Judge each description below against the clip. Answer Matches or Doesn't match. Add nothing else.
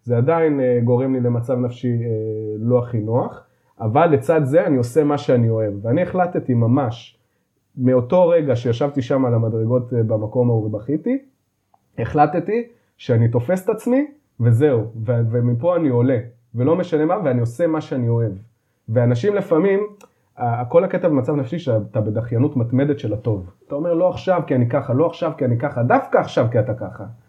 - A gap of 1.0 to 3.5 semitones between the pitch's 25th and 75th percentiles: Doesn't match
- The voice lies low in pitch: Matches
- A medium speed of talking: Matches